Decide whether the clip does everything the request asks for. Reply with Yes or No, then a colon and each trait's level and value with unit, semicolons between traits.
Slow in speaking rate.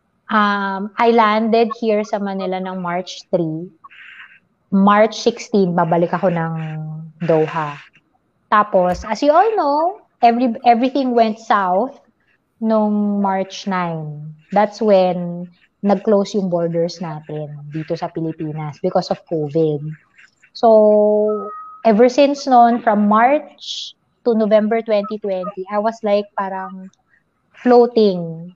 Yes: slow, 110 wpm